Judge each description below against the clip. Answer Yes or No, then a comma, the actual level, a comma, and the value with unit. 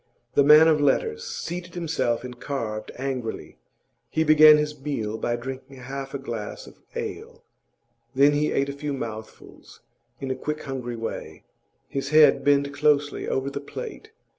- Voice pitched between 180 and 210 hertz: No, medium, 140 Hz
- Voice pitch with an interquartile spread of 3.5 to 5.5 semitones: No, average, 2.7 semitones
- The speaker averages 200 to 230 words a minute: No, average, 160 wpm